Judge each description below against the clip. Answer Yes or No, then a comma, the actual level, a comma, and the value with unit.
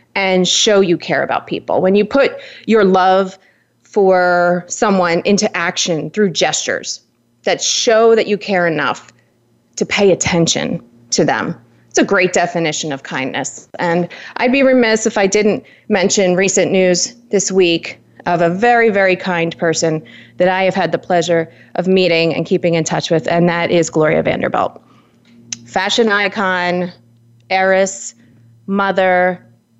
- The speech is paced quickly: No, average, 150 wpm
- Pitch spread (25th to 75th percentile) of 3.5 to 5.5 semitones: No, average, 3.1 semitones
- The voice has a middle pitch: Yes, medium, 180 Hz